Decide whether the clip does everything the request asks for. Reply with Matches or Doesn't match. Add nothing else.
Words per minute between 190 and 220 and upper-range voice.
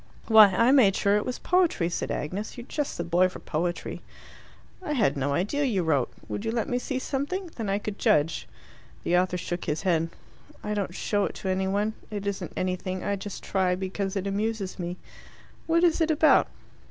Matches